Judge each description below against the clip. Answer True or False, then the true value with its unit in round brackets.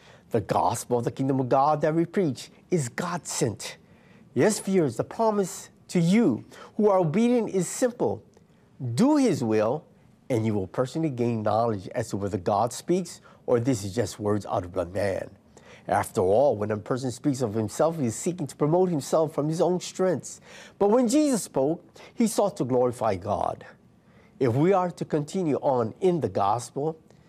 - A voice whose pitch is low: False (155 Hz)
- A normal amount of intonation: False (7.4 semitones)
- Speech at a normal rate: True (180 wpm)